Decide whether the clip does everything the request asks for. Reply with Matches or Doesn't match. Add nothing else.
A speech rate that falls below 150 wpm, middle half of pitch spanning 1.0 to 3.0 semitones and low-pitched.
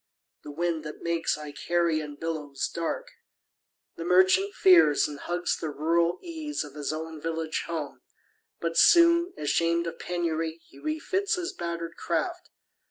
Doesn't match